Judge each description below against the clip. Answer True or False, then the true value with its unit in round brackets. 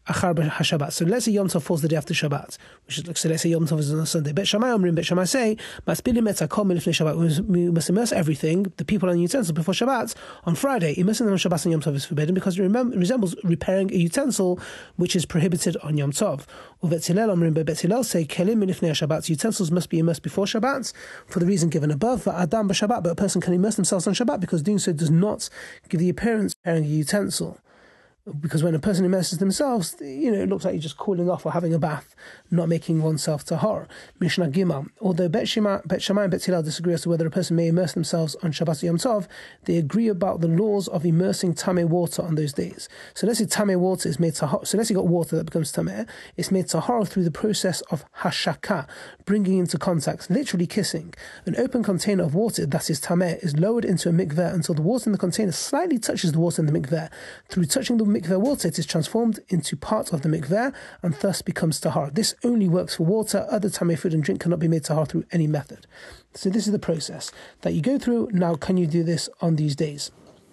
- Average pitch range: True (3.3 semitones)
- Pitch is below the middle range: False (180 Hz)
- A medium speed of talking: False (225 wpm)